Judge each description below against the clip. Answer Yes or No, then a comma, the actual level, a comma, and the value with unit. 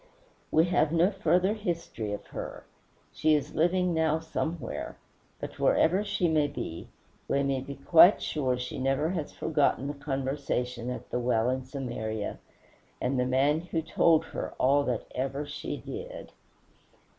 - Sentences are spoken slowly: No, average, 155 wpm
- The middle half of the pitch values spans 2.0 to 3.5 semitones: No, average, 4.3 semitones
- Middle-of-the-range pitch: Yes, medium, 145 Hz